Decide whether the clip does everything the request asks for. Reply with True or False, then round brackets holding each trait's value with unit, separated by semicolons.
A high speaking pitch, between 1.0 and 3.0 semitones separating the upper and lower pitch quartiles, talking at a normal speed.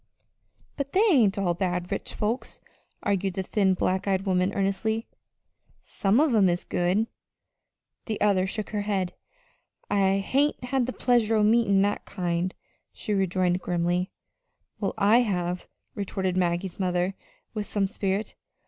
True (195 Hz; 2.7 semitones; 145 wpm)